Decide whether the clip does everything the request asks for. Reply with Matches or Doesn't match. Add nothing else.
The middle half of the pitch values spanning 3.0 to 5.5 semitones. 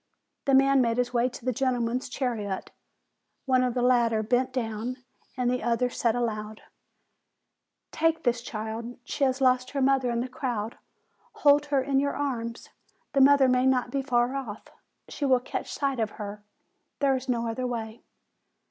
Doesn't match